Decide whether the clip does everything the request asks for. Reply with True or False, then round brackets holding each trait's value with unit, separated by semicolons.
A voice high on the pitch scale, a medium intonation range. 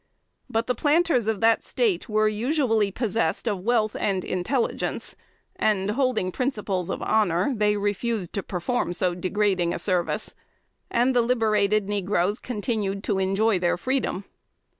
True (210 Hz; 3.5 semitones)